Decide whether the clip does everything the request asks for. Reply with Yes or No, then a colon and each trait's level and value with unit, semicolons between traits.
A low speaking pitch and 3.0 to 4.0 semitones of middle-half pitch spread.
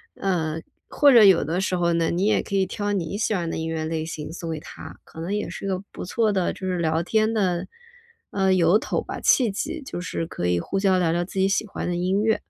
No: medium, 185 Hz; average, 3.5 semitones